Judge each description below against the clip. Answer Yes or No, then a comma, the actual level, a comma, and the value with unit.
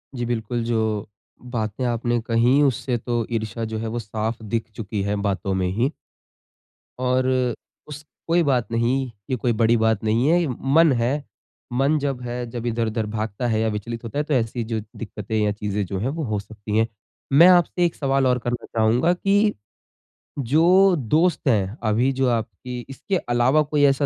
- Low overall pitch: Yes, low, 120 Hz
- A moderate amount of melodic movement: Yes, average, 3.6 semitones